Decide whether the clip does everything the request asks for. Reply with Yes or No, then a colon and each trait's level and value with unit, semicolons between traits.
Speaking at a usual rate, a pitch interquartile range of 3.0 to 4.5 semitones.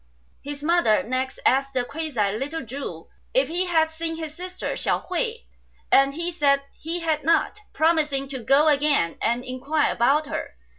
Yes: average, 165 wpm; average, 3.5 semitones